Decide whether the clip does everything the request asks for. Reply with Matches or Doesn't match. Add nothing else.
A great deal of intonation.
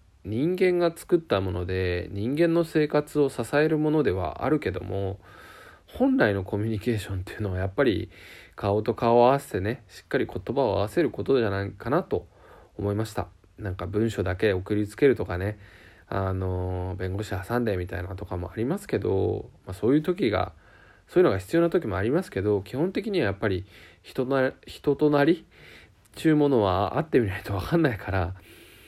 Matches